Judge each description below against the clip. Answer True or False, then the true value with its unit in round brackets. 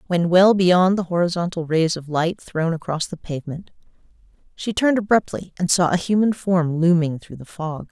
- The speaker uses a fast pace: False (180 wpm)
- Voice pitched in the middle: True (175 Hz)